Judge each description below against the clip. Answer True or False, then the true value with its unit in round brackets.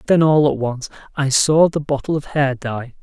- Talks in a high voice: False (140 Hz)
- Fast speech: True (220 wpm)